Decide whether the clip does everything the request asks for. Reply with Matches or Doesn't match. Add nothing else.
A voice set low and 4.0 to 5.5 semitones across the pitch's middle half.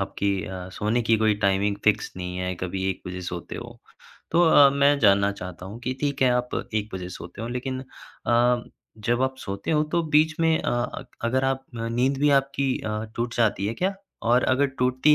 Matches